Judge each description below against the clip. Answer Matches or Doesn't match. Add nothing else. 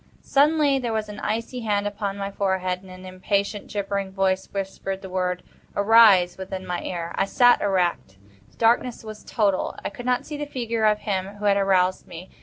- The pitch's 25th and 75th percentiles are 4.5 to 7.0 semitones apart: Doesn't match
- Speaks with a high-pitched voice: Matches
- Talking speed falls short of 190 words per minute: Doesn't match